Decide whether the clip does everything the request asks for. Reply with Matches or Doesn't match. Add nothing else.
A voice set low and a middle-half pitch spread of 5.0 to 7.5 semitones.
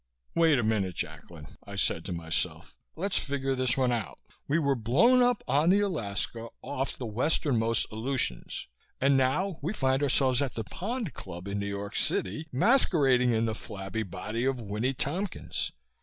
Matches